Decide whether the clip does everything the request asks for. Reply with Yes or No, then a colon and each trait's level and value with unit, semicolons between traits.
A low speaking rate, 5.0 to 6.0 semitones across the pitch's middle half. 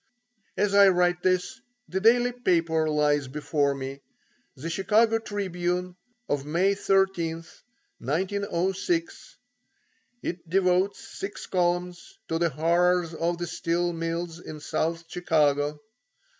No: slow, 115 wpm; average, 3.0 semitones